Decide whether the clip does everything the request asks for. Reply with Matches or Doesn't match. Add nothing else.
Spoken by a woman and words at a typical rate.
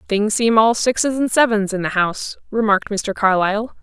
Matches